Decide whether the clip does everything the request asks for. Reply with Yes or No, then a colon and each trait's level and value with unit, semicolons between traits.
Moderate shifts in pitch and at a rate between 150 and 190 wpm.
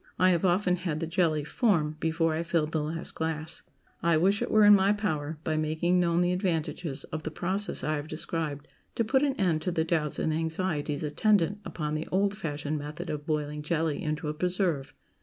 No: average, 3.0 semitones; fast, 205 wpm